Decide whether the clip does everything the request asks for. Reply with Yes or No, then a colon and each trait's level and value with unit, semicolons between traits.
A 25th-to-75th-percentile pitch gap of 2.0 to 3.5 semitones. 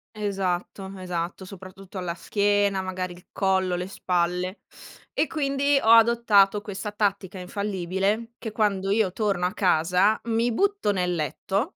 Yes: average, 2.7 semitones